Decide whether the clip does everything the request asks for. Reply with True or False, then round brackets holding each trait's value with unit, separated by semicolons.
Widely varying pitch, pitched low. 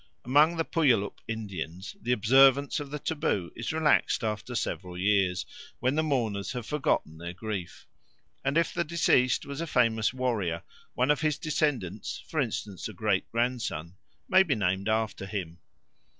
True (6.6 semitones; 115 Hz)